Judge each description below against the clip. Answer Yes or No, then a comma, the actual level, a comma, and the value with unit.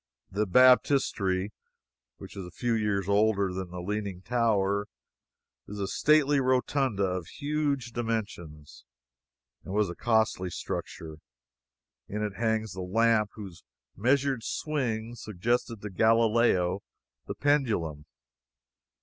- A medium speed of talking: No, slow, 115 wpm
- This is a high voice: No, low, 105 Hz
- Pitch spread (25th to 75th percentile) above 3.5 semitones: Yes, average, 4.0 semitones